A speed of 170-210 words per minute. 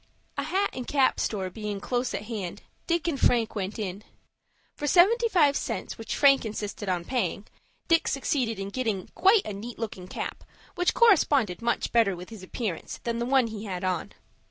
Yes: average, 185 wpm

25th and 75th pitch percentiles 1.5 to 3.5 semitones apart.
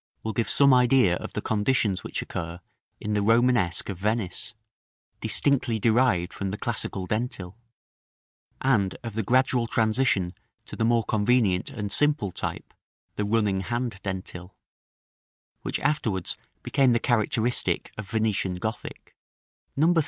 No: average, 3.9 semitones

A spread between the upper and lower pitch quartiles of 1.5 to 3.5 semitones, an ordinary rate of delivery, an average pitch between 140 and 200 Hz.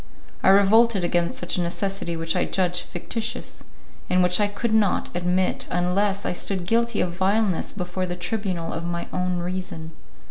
Yes: narrow, 2.4 semitones; average, 170 wpm; medium, 185 Hz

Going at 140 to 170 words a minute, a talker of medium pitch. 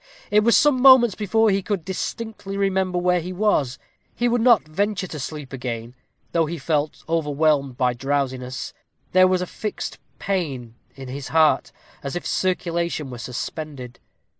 Yes: average, 160 wpm; medium, 165 Hz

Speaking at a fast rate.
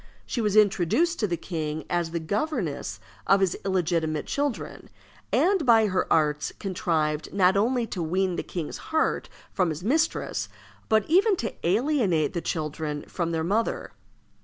No: average, 155 wpm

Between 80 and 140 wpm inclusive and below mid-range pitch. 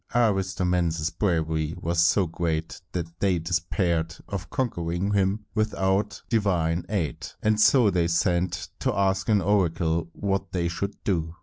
Yes: slow, 135 wpm; very low, 90 Hz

